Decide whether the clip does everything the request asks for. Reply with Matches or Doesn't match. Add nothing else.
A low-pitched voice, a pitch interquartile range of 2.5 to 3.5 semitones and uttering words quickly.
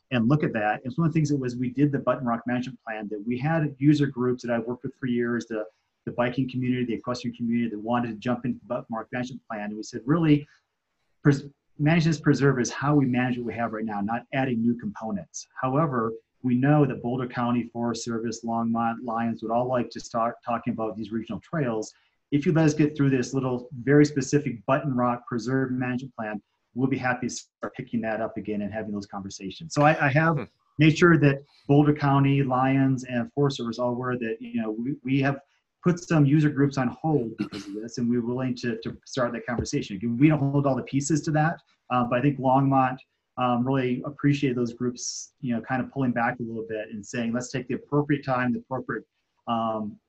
Matches